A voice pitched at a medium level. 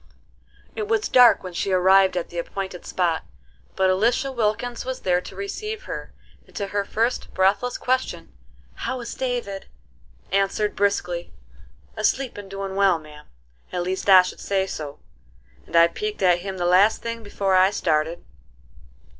No: high, 195 Hz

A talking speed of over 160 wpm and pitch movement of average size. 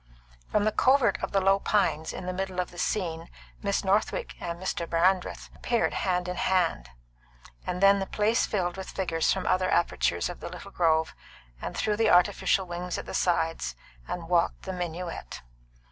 No: average, 180 wpm; narrow, 2.2 semitones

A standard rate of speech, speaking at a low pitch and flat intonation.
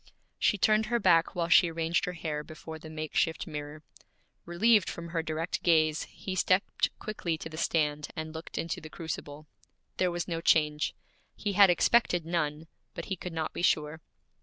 No: average, 180 wpm; medium, 165 Hz; narrow, 2.2 semitones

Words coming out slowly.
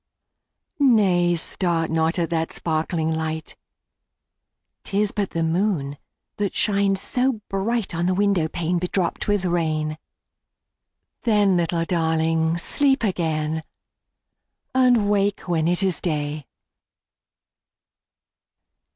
Yes: slow, 110 wpm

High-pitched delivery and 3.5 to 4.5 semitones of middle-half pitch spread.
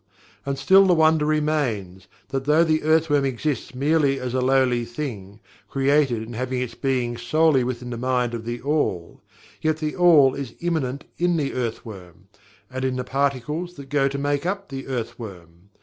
No: low, 135 Hz; average, 4.1 semitones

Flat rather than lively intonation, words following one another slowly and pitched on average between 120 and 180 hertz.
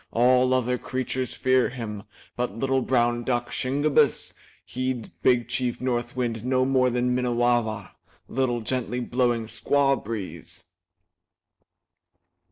Yes: narrow, 1.4 semitones; slow, 115 wpm; low, 125 Hz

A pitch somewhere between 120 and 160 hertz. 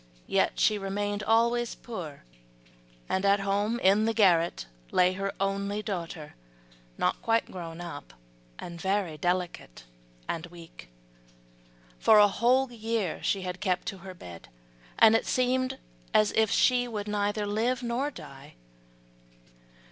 No: high, 200 Hz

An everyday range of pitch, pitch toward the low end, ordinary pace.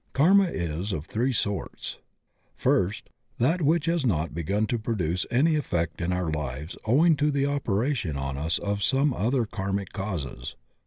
No: wide, 8.6 semitones; low, 100 Hz; average, 165 wpm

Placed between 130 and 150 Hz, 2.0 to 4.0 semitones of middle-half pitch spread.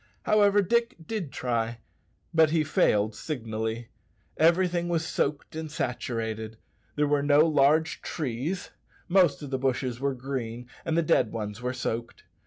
No: medium, 140 Hz; wide, 5.6 semitones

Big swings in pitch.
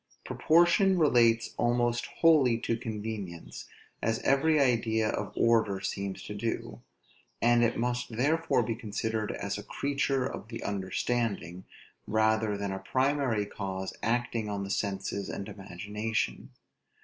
No: average, 3.2 semitones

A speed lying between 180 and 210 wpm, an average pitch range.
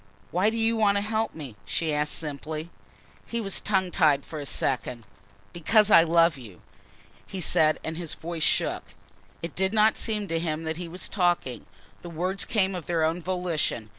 Yes: average, 190 wpm; average, 3.9 semitones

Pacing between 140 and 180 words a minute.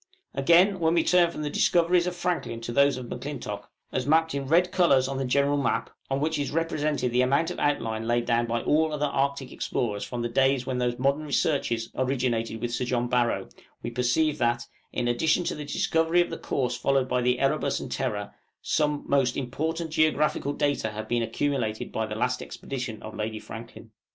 No: fast, 205 wpm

